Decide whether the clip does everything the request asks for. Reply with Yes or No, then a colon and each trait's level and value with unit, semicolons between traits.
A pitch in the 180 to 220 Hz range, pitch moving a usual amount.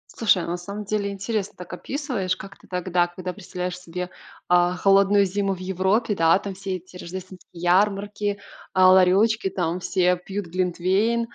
No: medium, 185 Hz; narrow, 1.9 semitones